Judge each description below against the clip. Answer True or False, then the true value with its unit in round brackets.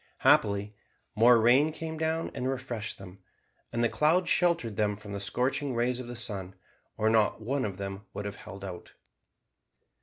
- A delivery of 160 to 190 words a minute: True (175 wpm)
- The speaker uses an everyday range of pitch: True (4.5 semitones)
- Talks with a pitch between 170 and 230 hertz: False (115 Hz)